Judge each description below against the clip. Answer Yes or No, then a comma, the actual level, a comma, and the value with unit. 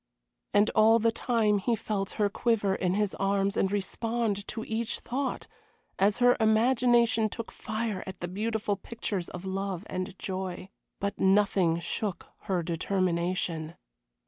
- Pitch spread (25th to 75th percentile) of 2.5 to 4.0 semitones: Yes, average, 3.0 semitones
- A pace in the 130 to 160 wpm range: Yes, average, 145 wpm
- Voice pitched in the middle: No, high, 200 Hz